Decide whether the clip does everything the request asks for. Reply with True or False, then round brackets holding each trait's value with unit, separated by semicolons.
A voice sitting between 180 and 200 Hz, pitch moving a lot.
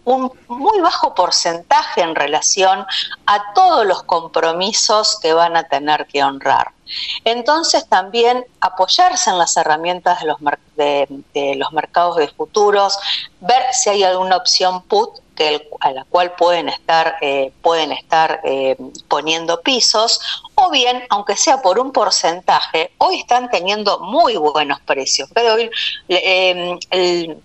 True (185 Hz; 7.1 semitones)